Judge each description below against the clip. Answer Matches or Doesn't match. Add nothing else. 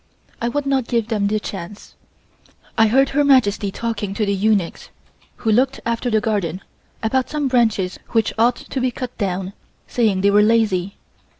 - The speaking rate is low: Doesn't match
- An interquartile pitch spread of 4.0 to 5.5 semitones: Doesn't match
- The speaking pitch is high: Matches